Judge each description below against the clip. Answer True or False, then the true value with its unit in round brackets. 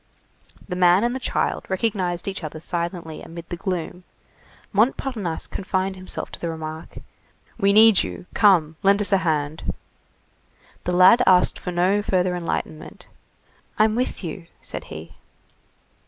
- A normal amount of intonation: True (3.0 semitones)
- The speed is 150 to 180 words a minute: False (140 wpm)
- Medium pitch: True (180 Hz)